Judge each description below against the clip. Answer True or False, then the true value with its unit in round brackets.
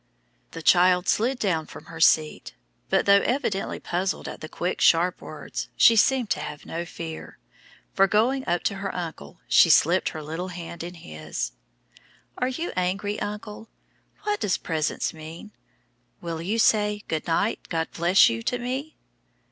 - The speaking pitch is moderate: True (180 Hz)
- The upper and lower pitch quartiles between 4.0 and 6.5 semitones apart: True (4.3 semitones)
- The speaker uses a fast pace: False (165 wpm)